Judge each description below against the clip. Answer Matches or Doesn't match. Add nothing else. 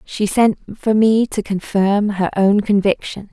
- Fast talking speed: Doesn't match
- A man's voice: Doesn't match